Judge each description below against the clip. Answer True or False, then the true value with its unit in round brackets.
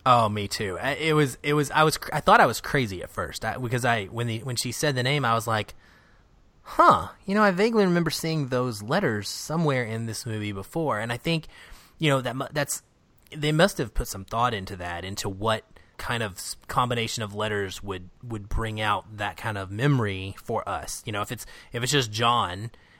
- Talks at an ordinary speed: False (215 wpm)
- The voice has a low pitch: True (120 Hz)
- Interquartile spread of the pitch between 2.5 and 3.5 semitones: False (5.5 semitones)